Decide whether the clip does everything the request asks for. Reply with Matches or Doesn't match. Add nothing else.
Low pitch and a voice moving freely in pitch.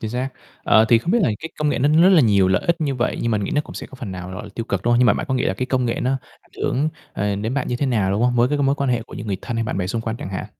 Doesn't match